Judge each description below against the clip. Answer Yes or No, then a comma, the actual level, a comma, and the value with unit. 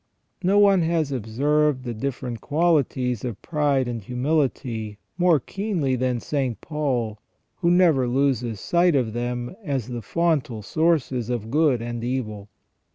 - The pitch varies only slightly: No, average, 4.7 semitones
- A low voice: Yes, low, 130 Hz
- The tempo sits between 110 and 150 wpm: Yes, average, 140 wpm